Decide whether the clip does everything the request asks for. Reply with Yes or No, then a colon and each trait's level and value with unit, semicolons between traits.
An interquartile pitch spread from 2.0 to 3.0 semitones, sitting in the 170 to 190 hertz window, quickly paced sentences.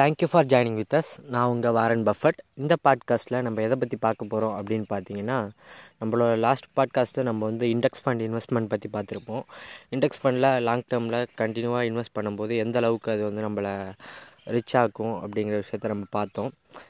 No: narrow, 2.6 semitones; low, 115 Hz; fast, 165 wpm